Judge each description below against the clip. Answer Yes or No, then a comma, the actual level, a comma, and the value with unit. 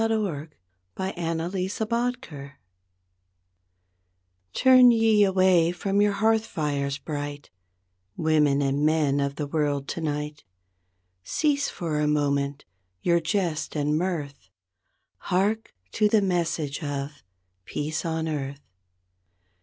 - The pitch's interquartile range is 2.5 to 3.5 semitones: No, average, 5.1 semitones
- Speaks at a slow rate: Yes, slow, 100 wpm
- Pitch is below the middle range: No, medium, 160 Hz